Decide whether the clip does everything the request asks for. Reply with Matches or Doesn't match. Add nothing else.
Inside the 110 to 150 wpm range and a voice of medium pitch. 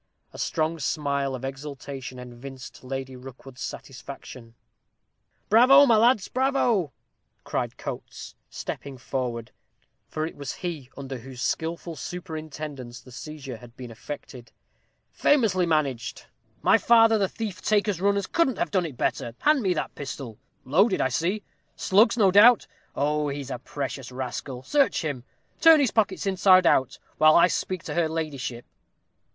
Matches